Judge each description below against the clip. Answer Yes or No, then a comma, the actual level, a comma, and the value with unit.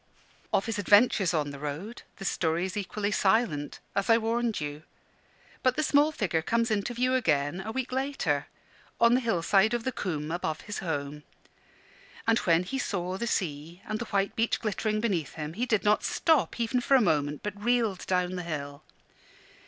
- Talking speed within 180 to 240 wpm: Yes, average, 185 wpm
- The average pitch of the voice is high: Yes, high, 200 Hz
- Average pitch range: No, wide, 6.1 semitones